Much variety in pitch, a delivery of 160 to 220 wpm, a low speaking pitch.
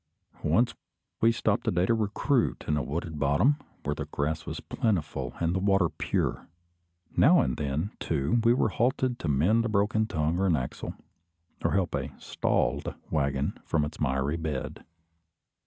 Yes: wide, 6.8 semitones; average, 170 wpm; very low, 85 Hz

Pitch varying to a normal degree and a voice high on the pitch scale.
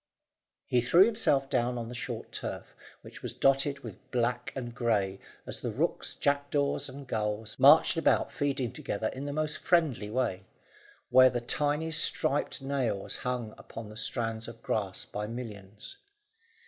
No: average, 4.2 semitones; low, 125 Hz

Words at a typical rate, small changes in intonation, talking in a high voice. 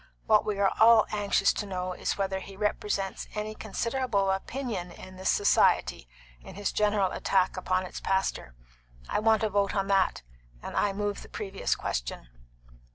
Yes: average, 165 wpm; narrow, 1.8 semitones; high, 200 Hz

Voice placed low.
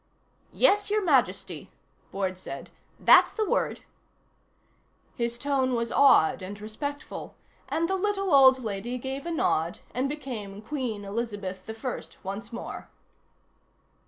No: high, 240 Hz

